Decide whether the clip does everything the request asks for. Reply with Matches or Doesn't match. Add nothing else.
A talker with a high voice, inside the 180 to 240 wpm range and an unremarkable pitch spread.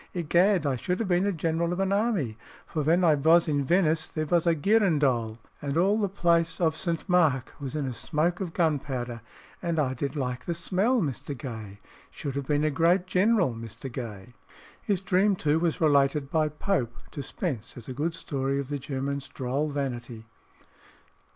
Doesn't match